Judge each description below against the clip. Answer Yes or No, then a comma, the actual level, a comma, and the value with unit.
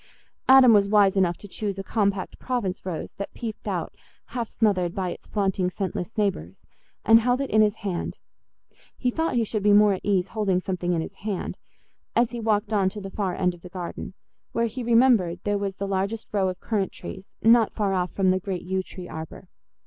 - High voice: Yes, high, 200 Hz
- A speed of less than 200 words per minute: No, fast, 205 wpm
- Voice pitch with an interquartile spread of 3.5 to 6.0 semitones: No, average, 2.9 semitones